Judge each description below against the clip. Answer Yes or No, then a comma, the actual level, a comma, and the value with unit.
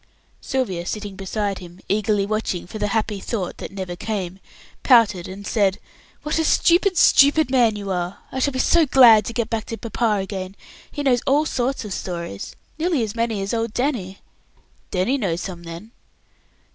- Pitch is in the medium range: No, high, 215 Hz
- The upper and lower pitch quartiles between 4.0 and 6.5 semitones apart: Yes, average, 4.6 semitones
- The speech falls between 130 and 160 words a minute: No, average, 180 wpm